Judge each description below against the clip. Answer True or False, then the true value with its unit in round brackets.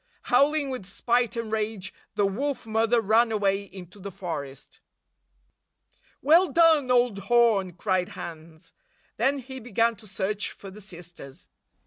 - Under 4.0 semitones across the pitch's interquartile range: False (4.3 semitones)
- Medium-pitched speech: False (215 Hz)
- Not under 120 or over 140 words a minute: True (135 wpm)